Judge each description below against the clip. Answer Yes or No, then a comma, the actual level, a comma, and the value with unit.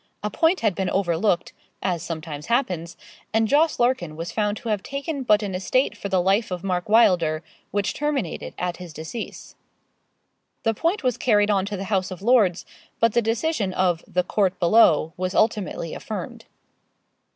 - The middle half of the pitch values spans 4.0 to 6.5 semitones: Yes, average, 4.4 semitones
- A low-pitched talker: No, high, 200 Hz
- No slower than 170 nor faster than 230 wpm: Yes, average, 175 wpm